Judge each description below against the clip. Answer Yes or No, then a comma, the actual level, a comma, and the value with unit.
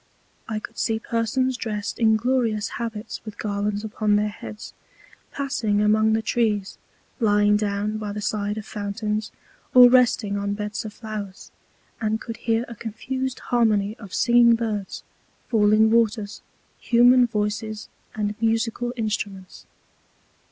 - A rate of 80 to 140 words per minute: Yes, slow, 135 wpm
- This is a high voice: Yes, high, 215 Hz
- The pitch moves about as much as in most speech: No, narrow, 1.8 semitones